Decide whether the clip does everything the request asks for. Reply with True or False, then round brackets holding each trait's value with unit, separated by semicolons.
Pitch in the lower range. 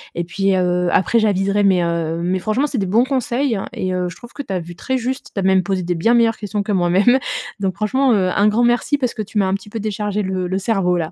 False (195 Hz)